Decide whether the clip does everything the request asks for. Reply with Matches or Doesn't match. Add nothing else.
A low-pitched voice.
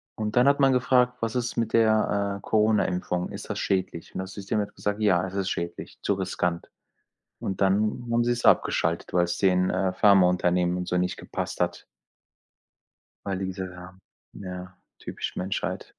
Matches